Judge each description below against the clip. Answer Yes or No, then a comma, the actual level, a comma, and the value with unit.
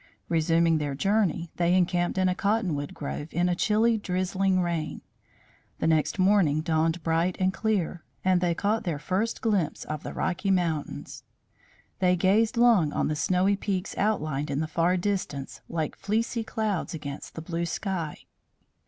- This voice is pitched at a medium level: Yes, medium, 180 Hz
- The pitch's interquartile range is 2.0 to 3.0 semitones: No, average, 3.5 semitones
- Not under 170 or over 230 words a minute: No, average, 160 wpm